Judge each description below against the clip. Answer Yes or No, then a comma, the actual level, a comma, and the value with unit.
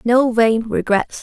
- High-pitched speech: Yes, high, 230 Hz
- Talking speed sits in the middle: Yes, average, 145 wpm